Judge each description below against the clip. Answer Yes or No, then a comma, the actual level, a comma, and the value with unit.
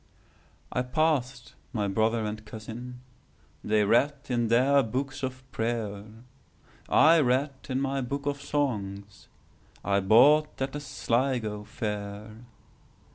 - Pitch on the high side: No, low, 125 Hz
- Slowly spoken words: Yes, slow, 105 wpm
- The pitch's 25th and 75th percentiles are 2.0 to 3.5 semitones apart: No, average, 4.1 semitones